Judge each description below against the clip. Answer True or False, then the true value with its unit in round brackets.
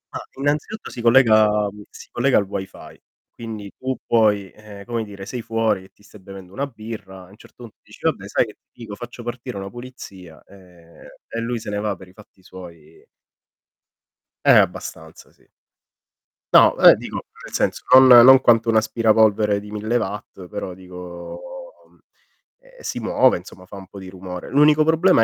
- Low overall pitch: True (105 Hz)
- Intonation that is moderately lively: True (3.7 semitones)